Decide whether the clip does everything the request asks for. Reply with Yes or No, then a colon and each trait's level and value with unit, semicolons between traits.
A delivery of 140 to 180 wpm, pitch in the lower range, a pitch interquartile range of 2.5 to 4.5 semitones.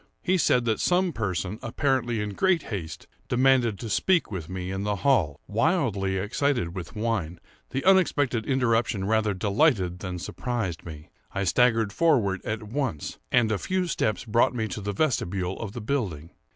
No: average, 165 wpm; low, 110 Hz; average, 5.3 semitones